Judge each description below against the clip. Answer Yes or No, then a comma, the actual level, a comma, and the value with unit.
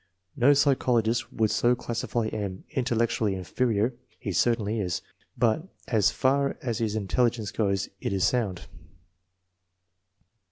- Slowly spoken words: Yes, slow, 125 wpm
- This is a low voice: Yes, low, 115 Hz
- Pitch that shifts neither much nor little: Yes, average, 3.2 semitones